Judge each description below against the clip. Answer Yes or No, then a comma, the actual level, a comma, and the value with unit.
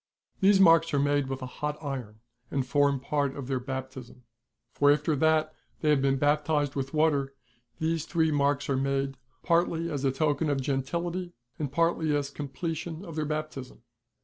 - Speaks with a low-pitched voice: No, medium, 145 Hz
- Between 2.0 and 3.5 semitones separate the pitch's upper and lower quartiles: Yes, average, 2.7 semitones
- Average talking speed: Yes, average, 175 wpm